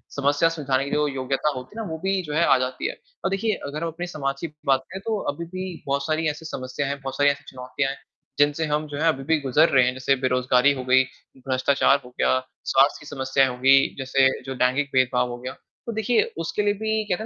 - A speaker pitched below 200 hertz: Yes, medium, 140 Hz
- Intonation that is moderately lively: Yes, average, 3.7 semitones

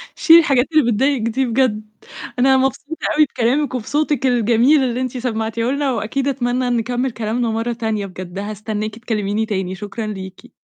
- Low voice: No, high, 235 Hz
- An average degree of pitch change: Yes, average, 3.6 semitones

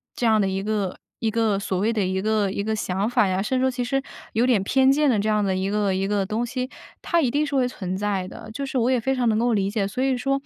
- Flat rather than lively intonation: No, average, 4.2 semitones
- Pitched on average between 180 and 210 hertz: No, high, 220 Hz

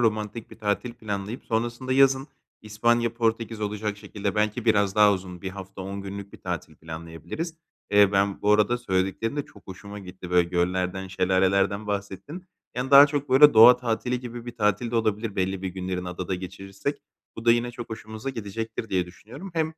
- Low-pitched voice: Yes, low, 105 Hz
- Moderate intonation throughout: Yes, average, 3.6 semitones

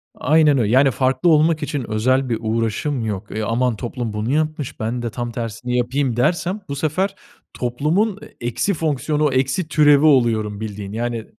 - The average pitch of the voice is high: No, low, 130 Hz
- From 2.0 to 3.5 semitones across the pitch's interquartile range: No, average, 4.7 semitones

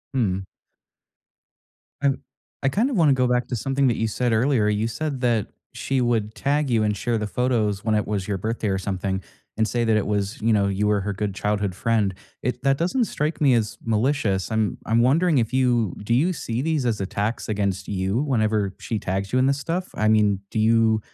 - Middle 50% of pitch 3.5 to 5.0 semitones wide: Yes, average, 3.9 semitones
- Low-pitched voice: Yes, low, 115 Hz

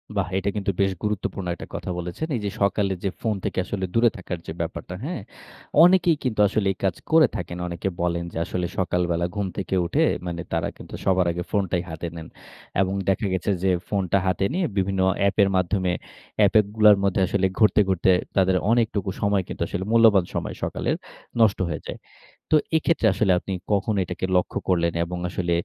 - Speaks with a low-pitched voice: Yes, very low, 95 Hz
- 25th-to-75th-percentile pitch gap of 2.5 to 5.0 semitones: Yes, average, 2.9 semitones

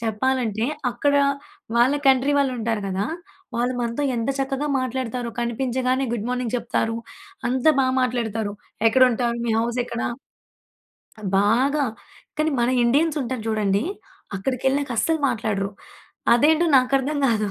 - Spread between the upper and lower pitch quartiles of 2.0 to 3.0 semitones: Yes, average, 2.7 semitones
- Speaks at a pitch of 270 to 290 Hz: No, high, 245 Hz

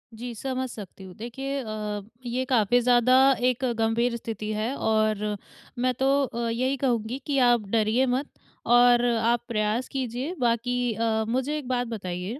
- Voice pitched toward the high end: Yes, high, 240 Hz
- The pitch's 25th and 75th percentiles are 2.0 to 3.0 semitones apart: Yes, narrow, 2.4 semitones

